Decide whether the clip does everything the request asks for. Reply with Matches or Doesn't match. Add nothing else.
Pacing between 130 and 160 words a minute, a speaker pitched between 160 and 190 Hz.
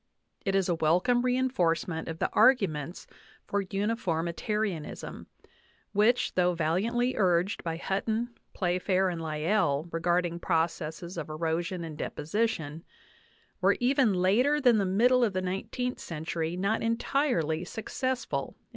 Matches